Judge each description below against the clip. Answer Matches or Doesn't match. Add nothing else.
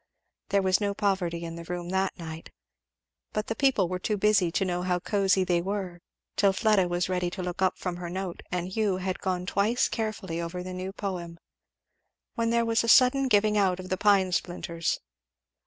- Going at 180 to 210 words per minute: Matches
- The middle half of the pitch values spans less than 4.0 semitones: Matches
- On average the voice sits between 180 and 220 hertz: Matches